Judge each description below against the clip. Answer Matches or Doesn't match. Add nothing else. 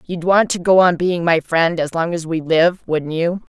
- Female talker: Matches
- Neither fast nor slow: Doesn't match